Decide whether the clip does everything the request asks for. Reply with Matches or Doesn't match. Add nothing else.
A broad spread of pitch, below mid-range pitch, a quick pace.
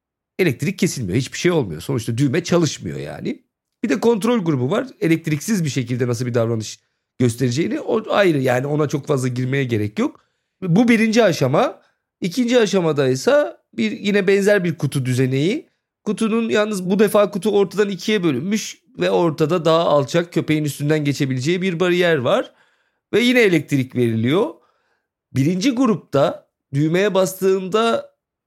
Doesn't match